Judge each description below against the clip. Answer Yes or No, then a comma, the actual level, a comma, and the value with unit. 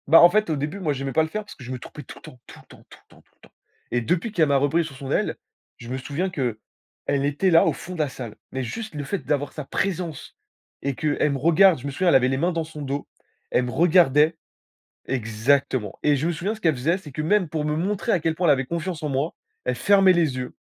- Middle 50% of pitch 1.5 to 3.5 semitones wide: No, average, 4.3 semitones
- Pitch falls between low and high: Yes, medium, 150 Hz